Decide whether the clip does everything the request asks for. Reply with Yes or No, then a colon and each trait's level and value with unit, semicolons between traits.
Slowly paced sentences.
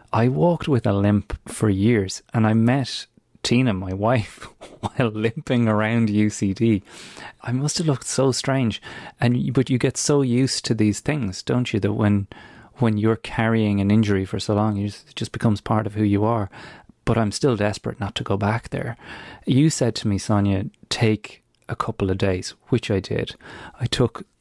No: average, 185 wpm